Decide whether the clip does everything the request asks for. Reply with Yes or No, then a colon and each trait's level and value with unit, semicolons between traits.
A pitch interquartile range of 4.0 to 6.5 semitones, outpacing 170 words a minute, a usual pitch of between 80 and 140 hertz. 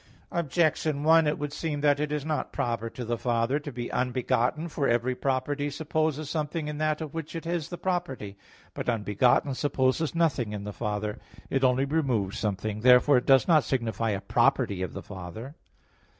Yes: average, 4.7 semitones; average, 185 wpm; low, 135 Hz